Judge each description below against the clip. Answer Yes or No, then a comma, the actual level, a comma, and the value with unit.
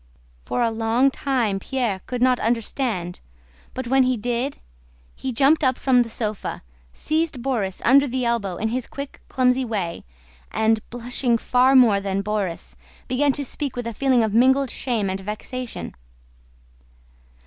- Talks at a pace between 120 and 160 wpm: Yes, average, 155 wpm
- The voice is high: Yes, high, 245 Hz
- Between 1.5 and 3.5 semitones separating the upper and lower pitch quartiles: Yes, average, 3.2 semitones